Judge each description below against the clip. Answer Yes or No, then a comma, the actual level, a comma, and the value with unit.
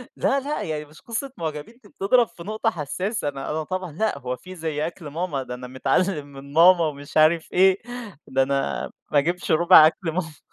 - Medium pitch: Yes, medium, 160 Hz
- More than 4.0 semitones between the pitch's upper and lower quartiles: Yes, average, 4.4 semitones